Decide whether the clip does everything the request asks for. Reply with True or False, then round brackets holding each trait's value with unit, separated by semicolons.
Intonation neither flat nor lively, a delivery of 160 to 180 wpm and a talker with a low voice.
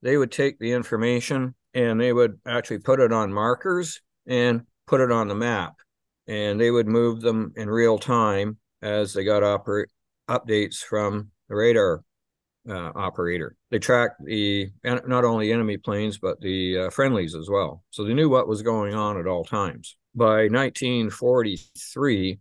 True (3.0 semitones; 165 wpm; 115 Hz)